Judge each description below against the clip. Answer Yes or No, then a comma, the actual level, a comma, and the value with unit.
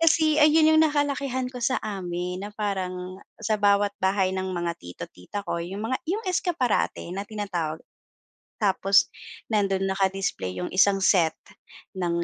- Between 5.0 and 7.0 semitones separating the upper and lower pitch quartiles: Yes, wide, 5.5 semitones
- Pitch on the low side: No, high, 200 Hz